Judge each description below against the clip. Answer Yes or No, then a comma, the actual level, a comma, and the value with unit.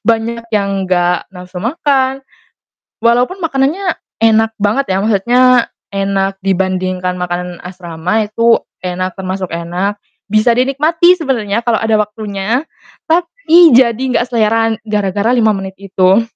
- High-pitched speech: Yes, high, 215 Hz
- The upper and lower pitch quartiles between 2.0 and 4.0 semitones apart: No, average, 4.4 semitones